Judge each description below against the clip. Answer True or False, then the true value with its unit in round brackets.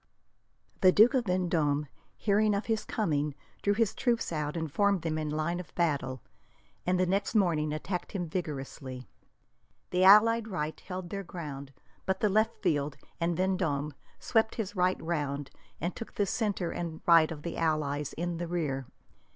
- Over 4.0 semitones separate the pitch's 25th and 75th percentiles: True (4.6 semitones)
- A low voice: False (175 Hz)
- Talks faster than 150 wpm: True (165 wpm)